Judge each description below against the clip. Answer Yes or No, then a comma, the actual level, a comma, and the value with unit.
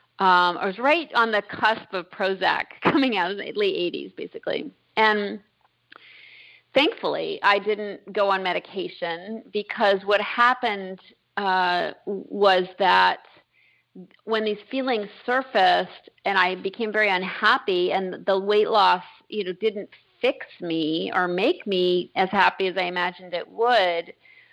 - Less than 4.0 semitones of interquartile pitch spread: No, average, 4.3 semitones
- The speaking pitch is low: No, high, 205 Hz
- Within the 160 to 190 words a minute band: No, average, 140 wpm